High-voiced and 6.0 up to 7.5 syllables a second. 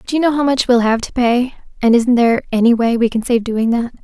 Yes: high, 240 Hz; 6.1 syllables/s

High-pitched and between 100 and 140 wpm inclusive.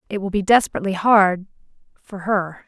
Yes: high, 195 Hz; slow, 135 wpm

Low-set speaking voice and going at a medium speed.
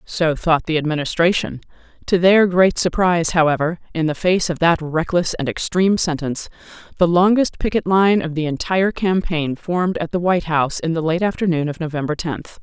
No: medium, 170 Hz; average, 180 wpm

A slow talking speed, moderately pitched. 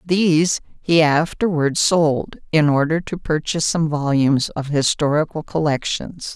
Yes: slow, 125 wpm; medium, 155 Hz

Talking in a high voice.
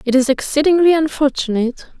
Yes: very high, 280 Hz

